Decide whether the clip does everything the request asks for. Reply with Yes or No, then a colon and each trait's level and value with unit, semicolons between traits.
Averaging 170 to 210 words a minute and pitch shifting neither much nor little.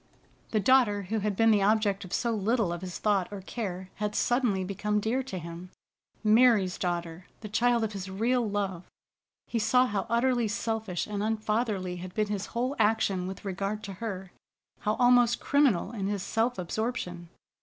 Yes: average, 175 wpm; average, 3.3 semitones